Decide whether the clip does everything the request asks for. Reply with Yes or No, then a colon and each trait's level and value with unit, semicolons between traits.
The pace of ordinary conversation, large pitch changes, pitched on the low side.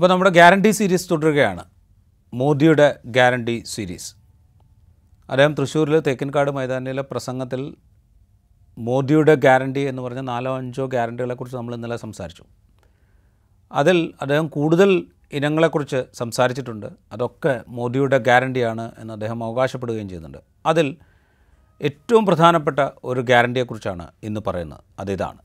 Yes: average, 100 wpm; wide, 5.8 semitones; low, 125 Hz